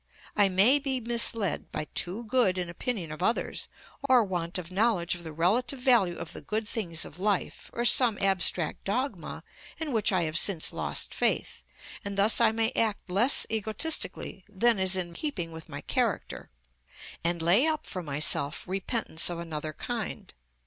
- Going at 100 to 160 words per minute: No, average, 170 wpm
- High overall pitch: Yes, high, 195 Hz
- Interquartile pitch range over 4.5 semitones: Yes, average, 5.2 semitones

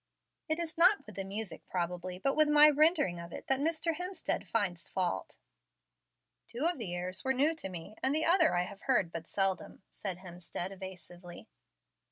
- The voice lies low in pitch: No, high, 195 Hz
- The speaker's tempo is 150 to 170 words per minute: No, average, 180 wpm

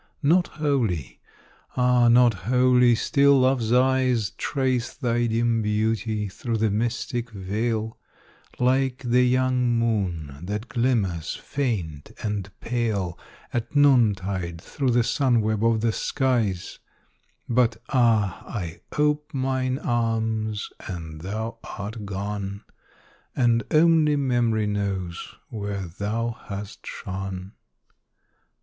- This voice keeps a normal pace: No, slow, 110 wpm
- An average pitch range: Yes, average, 3.7 semitones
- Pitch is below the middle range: Yes, low, 115 Hz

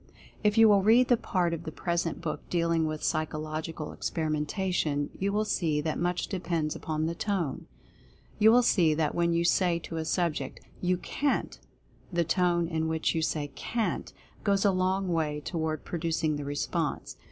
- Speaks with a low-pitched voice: No, medium, 170 Hz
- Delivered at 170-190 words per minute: Yes, average, 175 wpm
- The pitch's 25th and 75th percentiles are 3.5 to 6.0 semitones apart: No, average, 2.9 semitones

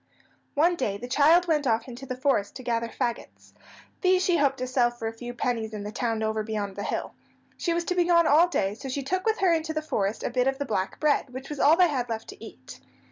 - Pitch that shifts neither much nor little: No, wide, 5.9 semitones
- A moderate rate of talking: No, fast, 260 wpm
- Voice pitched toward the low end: No, very high, 255 Hz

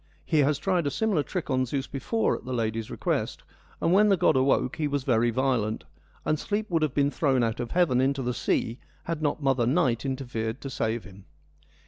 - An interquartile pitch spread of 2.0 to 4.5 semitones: Yes, average, 4.2 semitones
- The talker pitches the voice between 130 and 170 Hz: Yes, low, 135 Hz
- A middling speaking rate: No, fast, 210 wpm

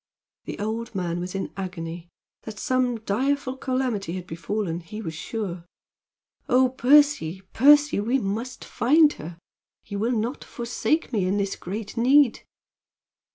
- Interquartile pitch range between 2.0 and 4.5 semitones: No, wide, 5.5 semitones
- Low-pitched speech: No, high, 220 Hz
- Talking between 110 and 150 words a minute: Yes, average, 140 wpm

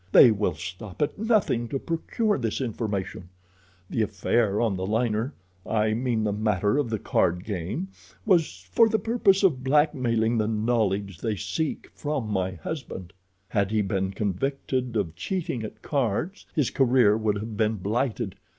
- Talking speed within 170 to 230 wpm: No, average, 150 wpm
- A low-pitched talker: Yes, low, 110 Hz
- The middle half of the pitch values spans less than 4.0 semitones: No, average, 5.0 semitones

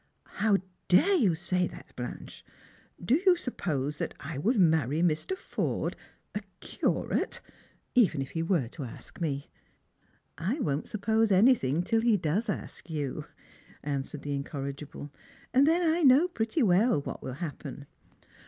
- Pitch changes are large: Yes, wide, 8.1 semitones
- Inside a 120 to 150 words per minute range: No, average, 160 wpm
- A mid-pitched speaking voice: Yes, medium, 175 Hz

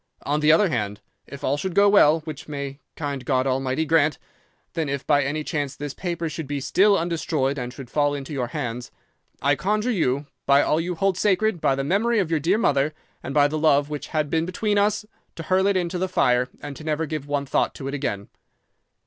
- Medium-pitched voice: Yes, medium, 150 Hz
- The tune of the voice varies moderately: Yes, average, 3.9 semitones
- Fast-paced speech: Yes, fast, 225 wpm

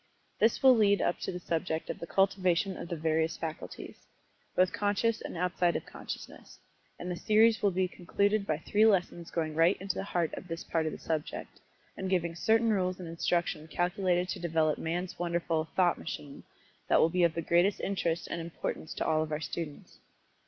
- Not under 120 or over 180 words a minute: No, average, 195 wpm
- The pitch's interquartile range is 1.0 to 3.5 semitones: Yes, average, 2.8 semitones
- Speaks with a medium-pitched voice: Yes, medium, 175 Hz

